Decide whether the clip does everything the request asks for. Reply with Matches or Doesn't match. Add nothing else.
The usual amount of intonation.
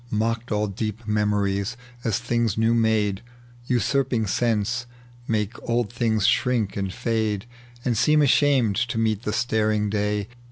Doesn't match